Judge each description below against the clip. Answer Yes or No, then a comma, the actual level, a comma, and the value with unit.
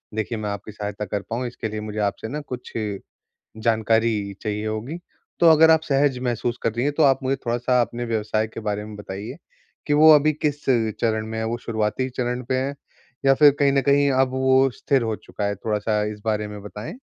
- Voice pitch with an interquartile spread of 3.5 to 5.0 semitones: Yes, average, 3.9 semitones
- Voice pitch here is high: No, low, 115 Hz